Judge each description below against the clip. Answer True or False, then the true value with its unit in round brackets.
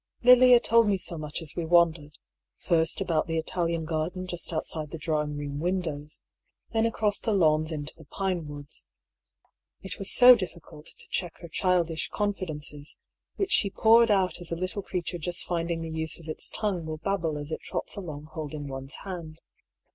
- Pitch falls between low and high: True (165 Hz)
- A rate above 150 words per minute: True (180 wpm)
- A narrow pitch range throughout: False (3.4 semitones)